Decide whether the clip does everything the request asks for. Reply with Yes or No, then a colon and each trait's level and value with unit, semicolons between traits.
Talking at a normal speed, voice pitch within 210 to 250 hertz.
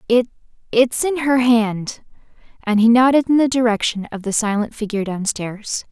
Yes: average, 150 wpm; high, 230 Hz